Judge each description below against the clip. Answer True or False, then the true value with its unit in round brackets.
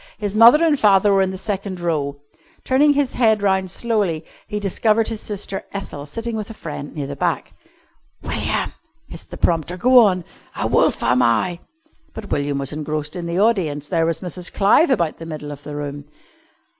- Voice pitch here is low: False (185 Hz)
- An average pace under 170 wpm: False (195 wpm)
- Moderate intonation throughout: False (6.0 semitones)